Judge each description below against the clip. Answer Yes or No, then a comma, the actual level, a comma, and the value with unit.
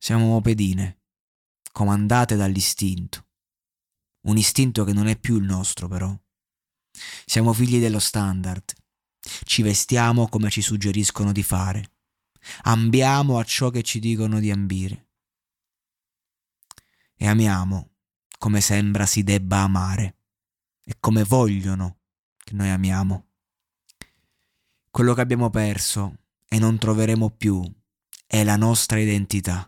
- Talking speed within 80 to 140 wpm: Yes, slow, 115 wpm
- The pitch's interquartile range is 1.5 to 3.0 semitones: Yes, average, 2.7 semitones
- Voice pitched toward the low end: Yes, low, 105 Hz